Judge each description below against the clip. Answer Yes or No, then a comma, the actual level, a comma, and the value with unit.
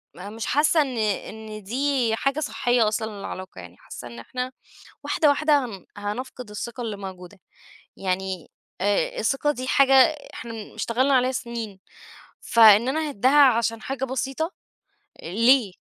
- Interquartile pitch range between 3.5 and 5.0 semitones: Yes, average, 4.5 semitones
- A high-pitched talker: Yes, high, 230 Hz